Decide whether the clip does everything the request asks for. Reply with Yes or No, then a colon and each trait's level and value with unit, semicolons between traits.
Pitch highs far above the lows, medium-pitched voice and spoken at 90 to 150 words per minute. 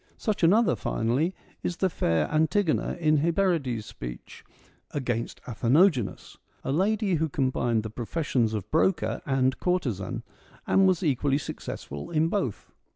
Yes: wide, 6.9 semitones; medium, 145 Hz; average, 140 wpm